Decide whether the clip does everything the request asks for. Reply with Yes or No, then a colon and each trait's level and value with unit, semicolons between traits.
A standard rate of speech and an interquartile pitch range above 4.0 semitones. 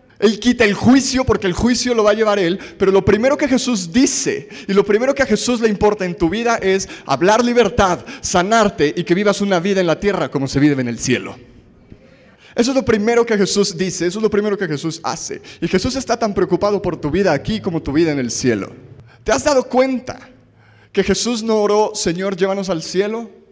No: fast, 225 wpm; average, 4.6 semitones